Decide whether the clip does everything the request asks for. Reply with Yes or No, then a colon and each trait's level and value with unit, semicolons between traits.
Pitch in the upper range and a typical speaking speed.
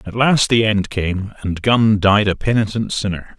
No: low, 105 Hz; average, 195 wpm